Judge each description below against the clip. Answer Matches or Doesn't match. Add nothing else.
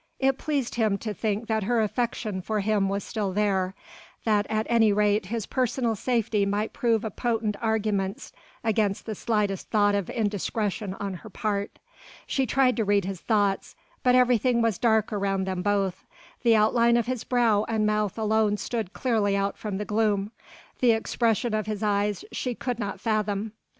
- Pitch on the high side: Matches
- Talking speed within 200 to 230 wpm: Doesn't match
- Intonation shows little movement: Matches